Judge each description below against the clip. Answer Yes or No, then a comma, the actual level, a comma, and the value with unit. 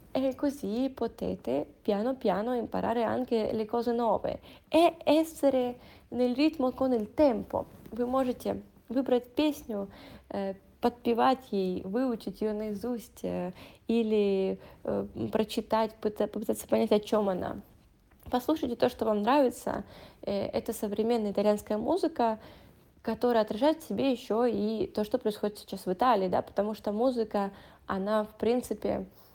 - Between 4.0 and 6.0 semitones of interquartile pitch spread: No, average, 3.3 semitones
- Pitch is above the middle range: Yes, high, 230 Hz